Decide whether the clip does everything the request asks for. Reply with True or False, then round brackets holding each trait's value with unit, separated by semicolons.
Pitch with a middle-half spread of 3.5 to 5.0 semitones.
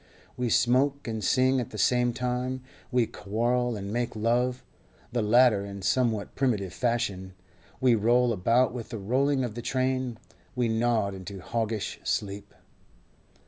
False (2.8 semitones)